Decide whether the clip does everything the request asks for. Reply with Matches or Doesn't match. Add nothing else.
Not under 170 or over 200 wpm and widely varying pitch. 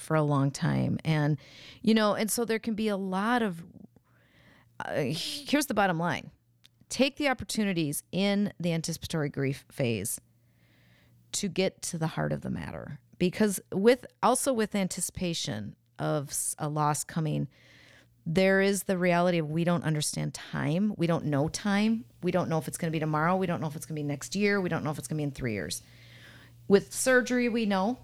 Matches